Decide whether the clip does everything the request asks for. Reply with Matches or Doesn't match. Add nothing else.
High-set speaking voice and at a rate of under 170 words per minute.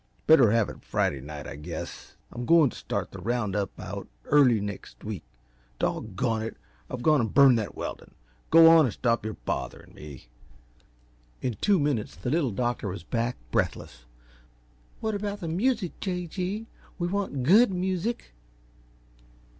Doesn't match